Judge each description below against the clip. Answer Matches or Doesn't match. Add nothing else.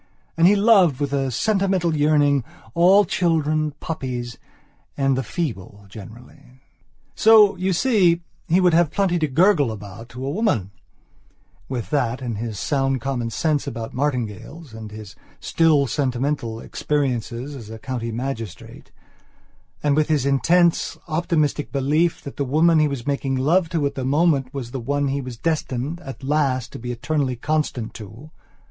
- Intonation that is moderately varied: Matches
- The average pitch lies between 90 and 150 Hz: Matches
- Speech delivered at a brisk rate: Doesn't match